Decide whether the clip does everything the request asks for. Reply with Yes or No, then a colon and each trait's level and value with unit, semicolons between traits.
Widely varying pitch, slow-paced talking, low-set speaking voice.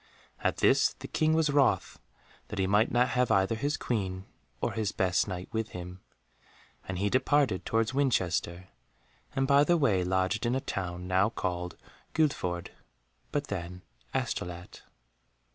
No: wide, 6.1 semitones; average, 150 wpm; low, 100 Hz